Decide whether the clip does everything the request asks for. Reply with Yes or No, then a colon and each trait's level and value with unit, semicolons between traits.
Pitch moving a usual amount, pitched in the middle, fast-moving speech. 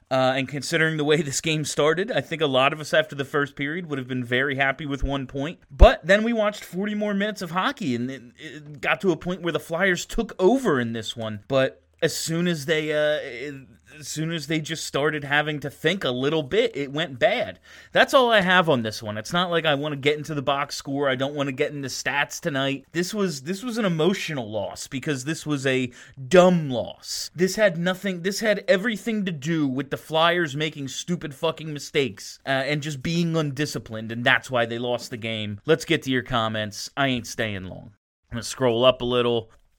Yes: average, 4.3 semitones; medium, 150 Hz; fast, 230 wpm